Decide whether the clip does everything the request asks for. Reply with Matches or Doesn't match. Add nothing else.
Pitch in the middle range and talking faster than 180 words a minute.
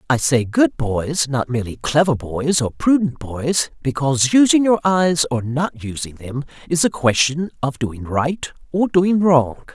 Doesn't match